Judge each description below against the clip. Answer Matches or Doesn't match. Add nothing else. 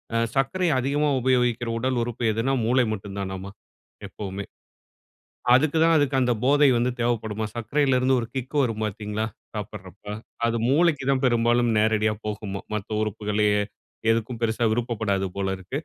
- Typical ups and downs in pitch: Matches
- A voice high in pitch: Doesn't match